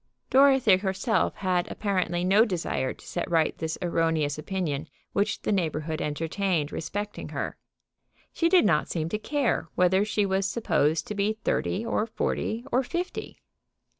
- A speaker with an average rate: Yes, average, 150 wpm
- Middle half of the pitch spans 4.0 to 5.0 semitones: Yes, average, 4.6 semitones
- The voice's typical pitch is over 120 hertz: Yes, high, 190 Hz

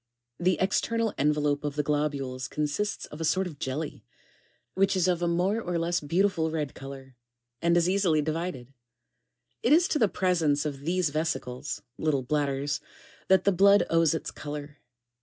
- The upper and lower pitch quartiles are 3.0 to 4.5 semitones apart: Yes, average, 4.0 semitones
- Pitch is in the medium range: Yes, medium, 160 Hz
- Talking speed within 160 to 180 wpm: Yes, average, 170 wpm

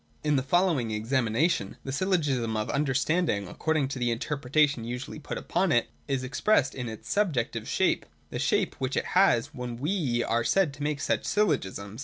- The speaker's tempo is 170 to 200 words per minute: Yes, average, 180 wpm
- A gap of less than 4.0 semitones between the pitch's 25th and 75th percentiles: No, average, 4.7 semitones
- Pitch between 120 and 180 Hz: Yes, low, 135 Hz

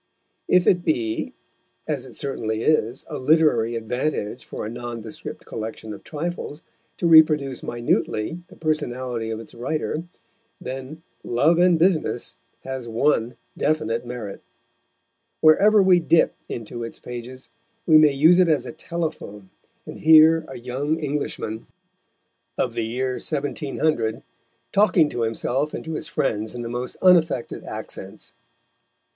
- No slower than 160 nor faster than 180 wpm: No, slow, 135 wpm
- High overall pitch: No, low, 135 Hz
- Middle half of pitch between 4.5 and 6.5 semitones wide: Yes, average, 5.3 semitones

